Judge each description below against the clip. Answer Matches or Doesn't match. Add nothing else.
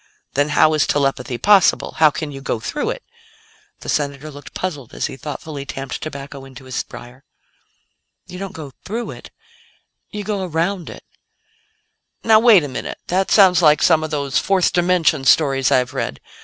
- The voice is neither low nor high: Matches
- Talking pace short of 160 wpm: Doesn't match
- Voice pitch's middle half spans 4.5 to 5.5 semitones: Matches